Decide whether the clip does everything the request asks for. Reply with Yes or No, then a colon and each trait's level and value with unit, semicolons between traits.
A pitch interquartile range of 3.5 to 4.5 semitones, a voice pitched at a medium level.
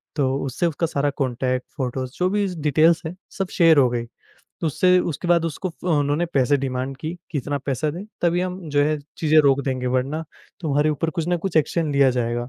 Yes: average, 4.0 semitones; medium, 150 Hz